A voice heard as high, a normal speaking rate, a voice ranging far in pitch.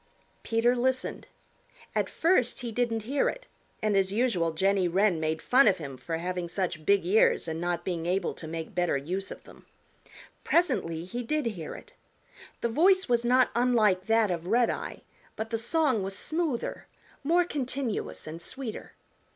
Yes: high, 215 Hz; average, 165 wpm; wide, 6.0 semitones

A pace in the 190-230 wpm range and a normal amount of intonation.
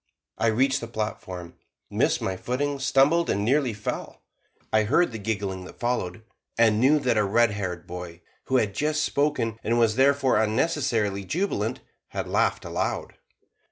No: average, 160 wpm; average, 4.9 semitones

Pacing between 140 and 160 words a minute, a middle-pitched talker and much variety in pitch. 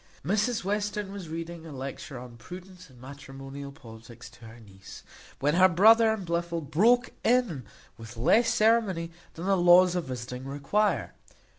Yes: average, 155 wpm; medium, 170 Hz; wide, 7.0 semitones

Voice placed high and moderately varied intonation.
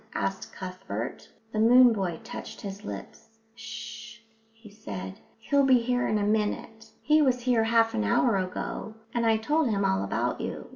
Yes: high, 220 Hz; average, 3.8 semitones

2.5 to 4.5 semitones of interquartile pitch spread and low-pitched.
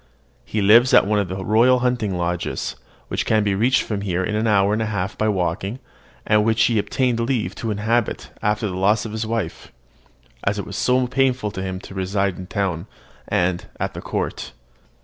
Yes: average, 3.0 semitones; low, 105 Hz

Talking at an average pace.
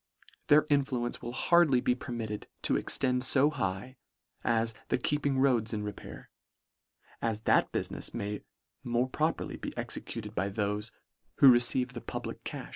Yes: average, 150 wpm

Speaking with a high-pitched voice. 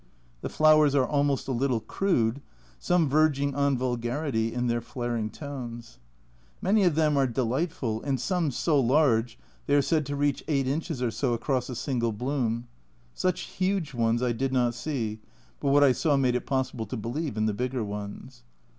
No: low, 130 Hz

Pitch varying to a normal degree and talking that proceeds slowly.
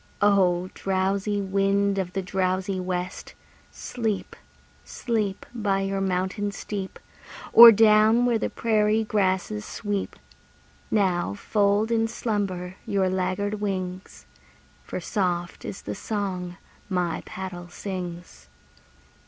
No: narrow, 2.2 semitones; slow, 110 wpm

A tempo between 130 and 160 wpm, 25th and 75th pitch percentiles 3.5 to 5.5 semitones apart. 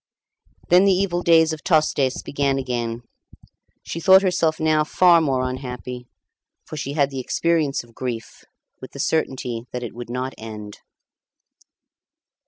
Yes: average, 145 wpm; average, 4.6 semitones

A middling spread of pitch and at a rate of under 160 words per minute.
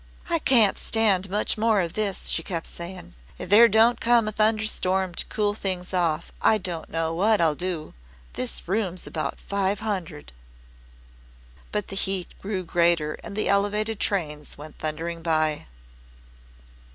Yes: average, 4.0 semitones; average, 150 wpm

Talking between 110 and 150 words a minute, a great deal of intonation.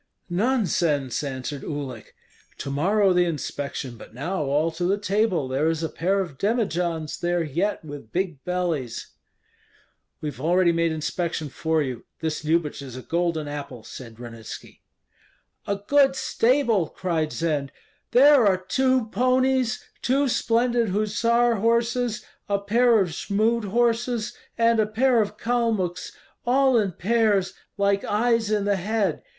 Yes: average, 145 wpm; wide, 6.6 semitones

